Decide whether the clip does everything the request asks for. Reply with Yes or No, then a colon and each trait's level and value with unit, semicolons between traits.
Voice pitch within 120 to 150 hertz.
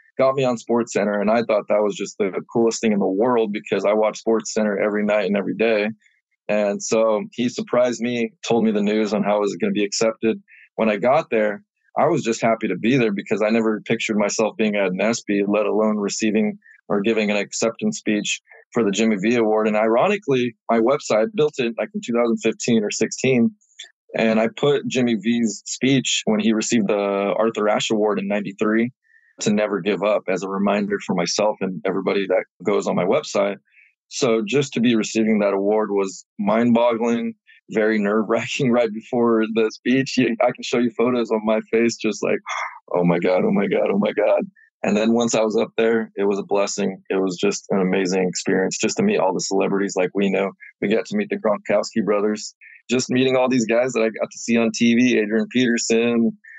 No: low, 110 Hz